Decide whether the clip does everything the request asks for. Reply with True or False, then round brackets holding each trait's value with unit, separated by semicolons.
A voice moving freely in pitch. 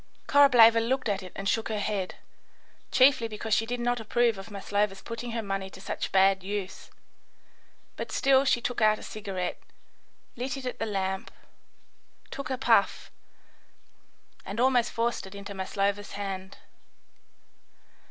False (3.6 semitones)